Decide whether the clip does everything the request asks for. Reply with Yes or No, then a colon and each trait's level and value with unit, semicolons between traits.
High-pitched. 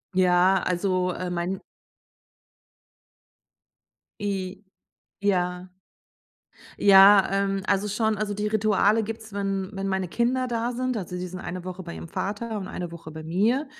Yes: high, 195 Hz